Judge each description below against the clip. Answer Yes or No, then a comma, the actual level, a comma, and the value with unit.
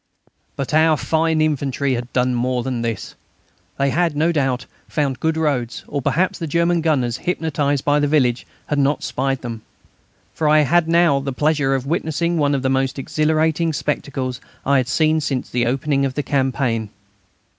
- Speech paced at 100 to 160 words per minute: No, average, 175 wpm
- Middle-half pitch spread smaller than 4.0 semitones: Yes, average, 3.3 semitones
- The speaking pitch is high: No, medium, 140 Hz